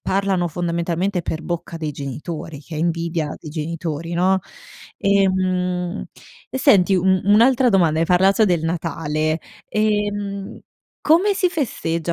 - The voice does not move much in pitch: No, average, 3.3 semitones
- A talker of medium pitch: Yes, medium, 180 Hz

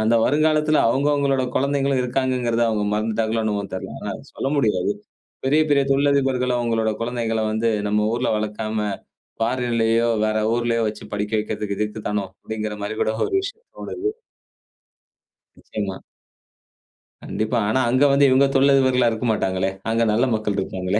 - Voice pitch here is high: No, low, 115 Hz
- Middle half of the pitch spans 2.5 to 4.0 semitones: Yes, average, 3.7 semitones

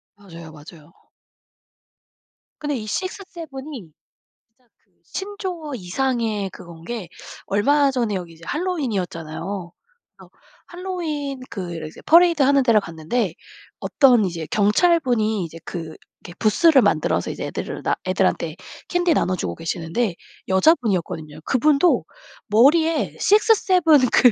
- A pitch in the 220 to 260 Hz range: Yes, high, 235 Hz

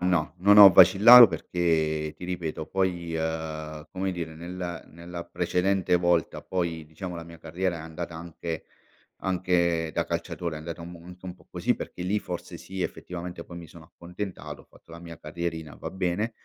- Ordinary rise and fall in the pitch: No, narrow, 1.8 semitones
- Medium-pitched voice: No, very low, 85 Hz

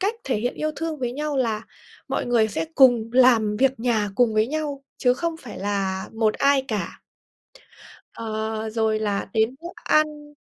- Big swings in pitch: No, average, 4.3 semitones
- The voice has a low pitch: No, high, 235 Hz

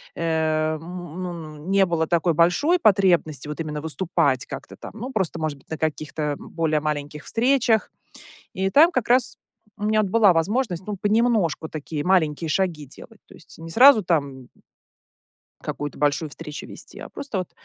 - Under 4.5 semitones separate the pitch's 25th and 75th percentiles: No, average, 5.0 semitones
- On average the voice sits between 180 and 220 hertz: No, medium, 165 Hz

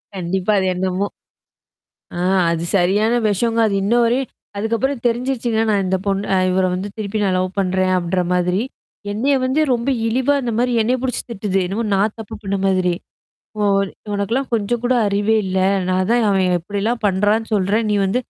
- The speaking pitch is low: No, high, 205 Hz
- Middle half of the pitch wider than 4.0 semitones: No, average, 3.7 semitones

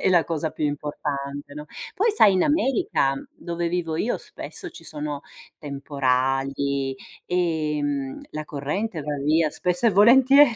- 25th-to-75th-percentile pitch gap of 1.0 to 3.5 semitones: No, average, 4.7 semitones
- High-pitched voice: No, medium, 155 Hz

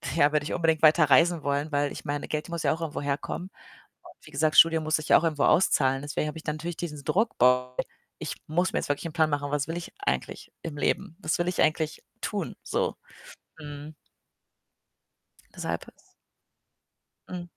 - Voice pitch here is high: No, medium, 155 Hz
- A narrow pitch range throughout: Yes, narrow, 2.3 semitones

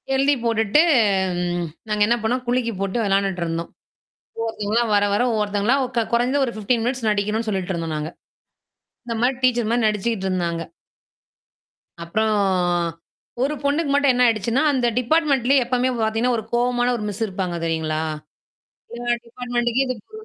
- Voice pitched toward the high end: Yes, high, 230 Hz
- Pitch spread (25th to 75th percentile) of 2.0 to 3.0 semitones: No, average, 3.6 semitones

